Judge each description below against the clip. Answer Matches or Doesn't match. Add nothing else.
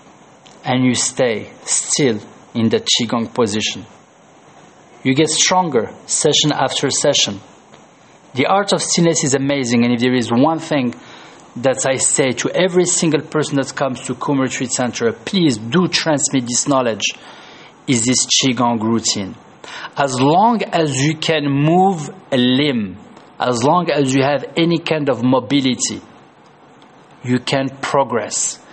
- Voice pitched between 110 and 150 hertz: Matches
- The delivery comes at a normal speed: Doesn't match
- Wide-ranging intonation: Doesn't match